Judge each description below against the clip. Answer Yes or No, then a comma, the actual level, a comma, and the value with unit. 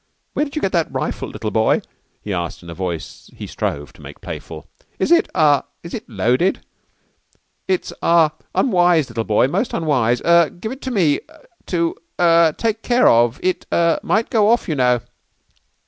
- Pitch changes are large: Yes, wide, 7.9 semitones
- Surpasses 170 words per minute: Yes, average, 180 wpm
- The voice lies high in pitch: No, medium, 165 Hz